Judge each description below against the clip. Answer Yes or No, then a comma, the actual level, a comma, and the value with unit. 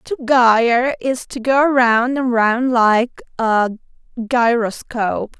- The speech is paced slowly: Yes, slow, 120 wpm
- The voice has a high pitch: Yes, high, 240 Hz